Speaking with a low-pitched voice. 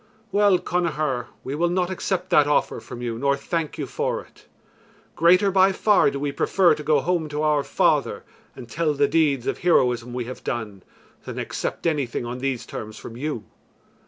No: medium, 150 Hz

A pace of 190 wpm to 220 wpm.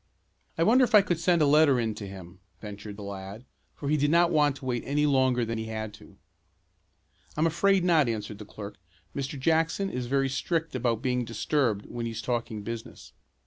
Yes: average, 200 wpm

